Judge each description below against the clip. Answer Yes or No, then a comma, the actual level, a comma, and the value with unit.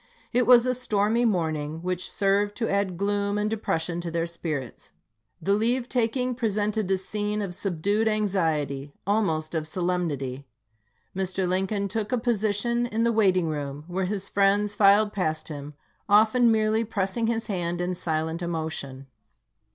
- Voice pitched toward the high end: Yes, high, 195 Hz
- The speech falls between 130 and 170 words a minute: Yes, average, 150 wpm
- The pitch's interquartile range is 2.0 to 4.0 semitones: No, average, 4.4 semitones